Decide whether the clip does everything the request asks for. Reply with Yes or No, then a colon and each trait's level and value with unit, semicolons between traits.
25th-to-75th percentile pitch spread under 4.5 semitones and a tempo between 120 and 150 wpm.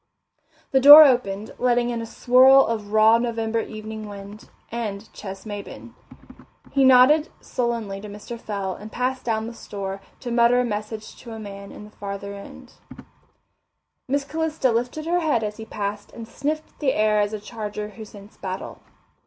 No: average, 3.2 semitones; average, 170 wpm